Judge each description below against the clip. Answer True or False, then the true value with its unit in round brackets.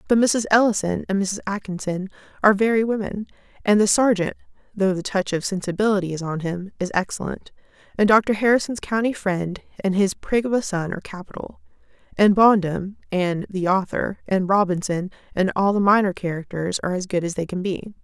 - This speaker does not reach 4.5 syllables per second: False (5.5 syllables/s)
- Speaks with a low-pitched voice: False (195 Hz)